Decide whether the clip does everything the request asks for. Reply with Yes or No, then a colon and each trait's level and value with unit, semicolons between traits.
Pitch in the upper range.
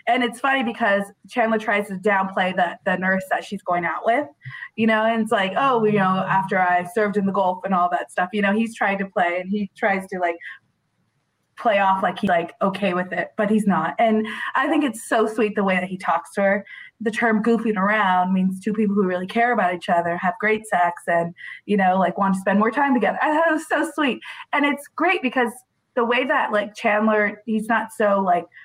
Yes: high, 205 Hz